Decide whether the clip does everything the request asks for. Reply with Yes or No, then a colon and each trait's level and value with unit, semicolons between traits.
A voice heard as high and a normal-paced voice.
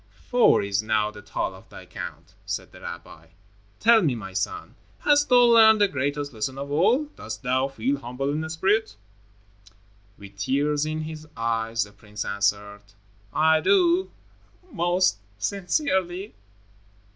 No: medium, 145 Hz; average, 145 wpm